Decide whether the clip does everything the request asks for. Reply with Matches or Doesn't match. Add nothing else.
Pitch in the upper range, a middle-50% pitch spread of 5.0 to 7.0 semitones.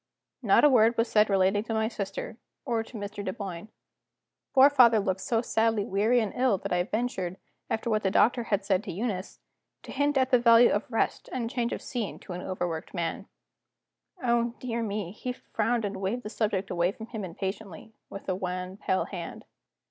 Doesn't match